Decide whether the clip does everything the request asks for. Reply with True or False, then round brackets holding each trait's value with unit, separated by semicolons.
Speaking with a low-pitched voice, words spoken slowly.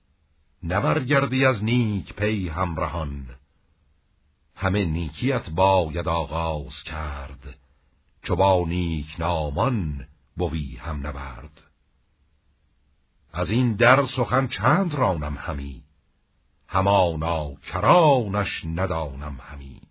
True (80 Hz; 85 wpm)